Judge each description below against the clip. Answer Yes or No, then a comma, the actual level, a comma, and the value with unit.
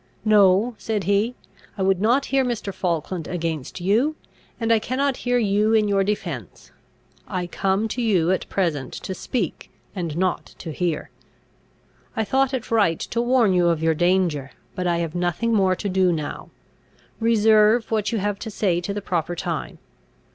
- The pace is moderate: Yes, average, 175 wpm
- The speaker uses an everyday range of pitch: Yes, average, 4.2 semitones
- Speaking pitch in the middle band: No, high, 195 Hz